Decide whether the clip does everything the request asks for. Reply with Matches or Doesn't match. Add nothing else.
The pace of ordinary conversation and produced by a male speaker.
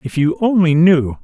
Matches